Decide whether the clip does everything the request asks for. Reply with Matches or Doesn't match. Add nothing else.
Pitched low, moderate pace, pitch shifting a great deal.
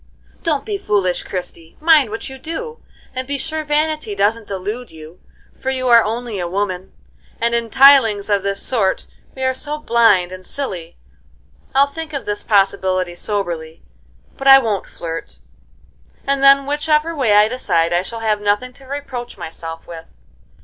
Doesn't match